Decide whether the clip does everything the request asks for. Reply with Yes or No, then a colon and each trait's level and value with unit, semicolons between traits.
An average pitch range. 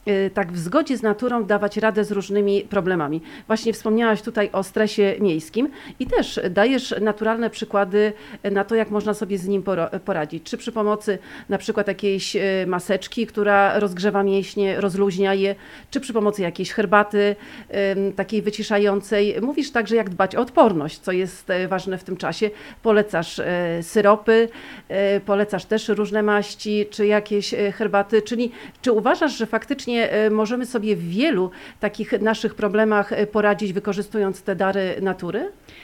No: narrow, 2.0 semitones